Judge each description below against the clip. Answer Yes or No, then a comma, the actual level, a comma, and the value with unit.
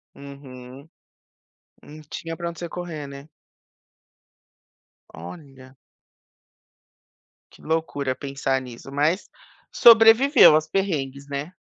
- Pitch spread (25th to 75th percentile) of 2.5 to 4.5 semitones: Yes, average, 3.7 semitones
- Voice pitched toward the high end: No, medium, 145 Hz